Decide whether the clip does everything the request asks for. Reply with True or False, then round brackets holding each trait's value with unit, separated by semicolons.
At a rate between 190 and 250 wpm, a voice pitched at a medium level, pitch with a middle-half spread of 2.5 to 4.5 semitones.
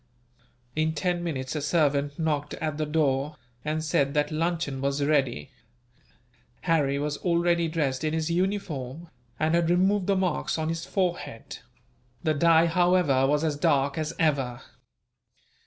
False (145 wpm; 155 Hz; 2.9 semitones)